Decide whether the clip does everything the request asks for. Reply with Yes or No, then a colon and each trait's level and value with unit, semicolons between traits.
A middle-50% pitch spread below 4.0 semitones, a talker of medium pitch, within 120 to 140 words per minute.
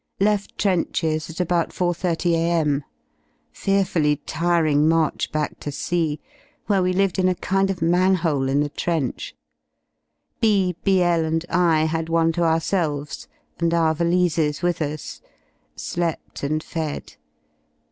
Yes: narrow, 2.5 semitones; medium, 165 Hz; slow, 135 wpm